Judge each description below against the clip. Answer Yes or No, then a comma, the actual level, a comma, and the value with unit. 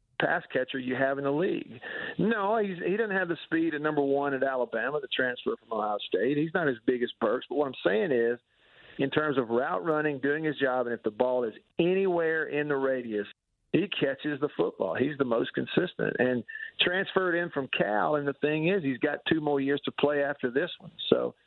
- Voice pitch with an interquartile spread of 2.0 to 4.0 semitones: Yes, average, 3.6 semitones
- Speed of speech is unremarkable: No, fast, 225 wpm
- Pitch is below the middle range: No, medium, 145 Hz